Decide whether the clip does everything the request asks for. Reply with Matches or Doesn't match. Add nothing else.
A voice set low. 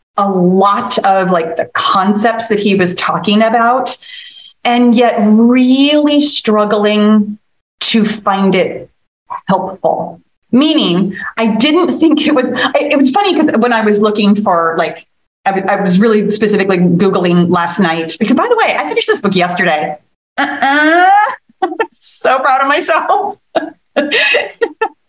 Doesn't match